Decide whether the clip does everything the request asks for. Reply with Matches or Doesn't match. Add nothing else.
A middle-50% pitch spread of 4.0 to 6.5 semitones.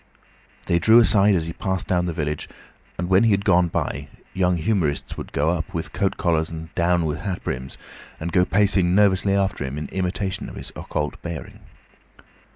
Doesn't match